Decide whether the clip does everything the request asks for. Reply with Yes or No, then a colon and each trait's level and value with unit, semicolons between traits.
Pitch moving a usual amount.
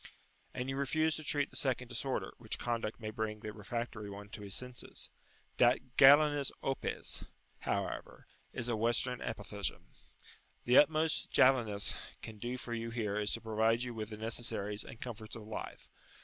Yes: average, 3.0 semitones